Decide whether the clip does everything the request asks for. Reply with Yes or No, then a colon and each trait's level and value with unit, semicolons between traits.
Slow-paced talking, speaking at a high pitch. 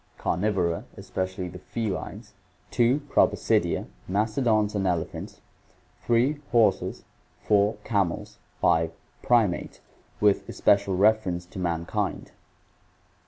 No: slow, 90 wpm; low, 100 Hz